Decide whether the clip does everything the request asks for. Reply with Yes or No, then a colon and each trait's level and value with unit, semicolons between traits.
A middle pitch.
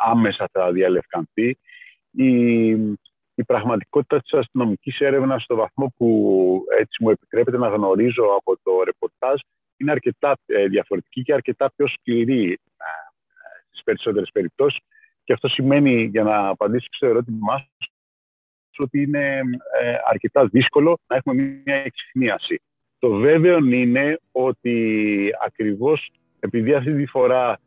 No: low, 130 Hz